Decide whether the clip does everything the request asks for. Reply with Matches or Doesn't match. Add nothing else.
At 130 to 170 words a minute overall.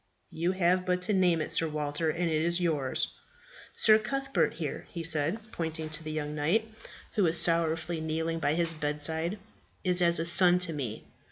Doesn't match